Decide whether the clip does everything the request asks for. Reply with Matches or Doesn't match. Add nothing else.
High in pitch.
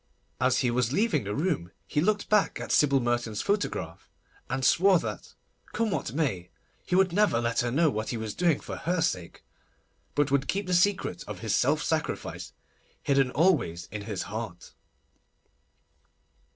Doesn't match